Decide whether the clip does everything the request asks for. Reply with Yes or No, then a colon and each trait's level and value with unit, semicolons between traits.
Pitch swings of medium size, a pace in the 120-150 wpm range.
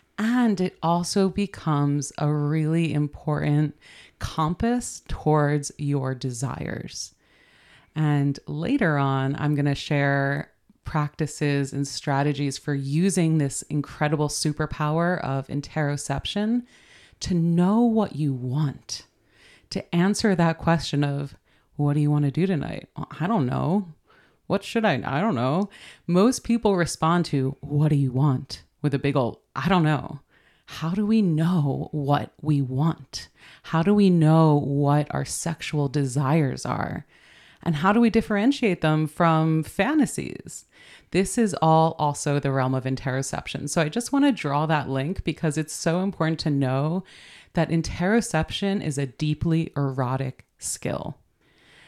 Yes: average, 3.3 semitones; average, 140 wpm